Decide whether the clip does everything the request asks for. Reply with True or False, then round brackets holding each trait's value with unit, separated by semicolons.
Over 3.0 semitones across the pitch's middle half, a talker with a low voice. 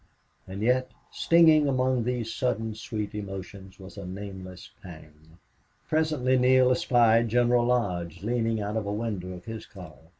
True (4.6 semitones; 110 Hz)